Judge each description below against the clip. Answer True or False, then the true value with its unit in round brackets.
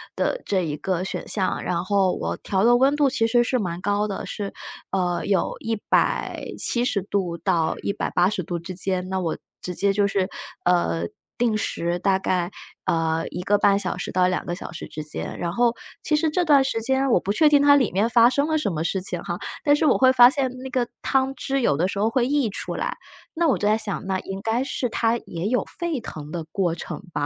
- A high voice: True (200 Hz)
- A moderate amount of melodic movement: False (5.8 semitones)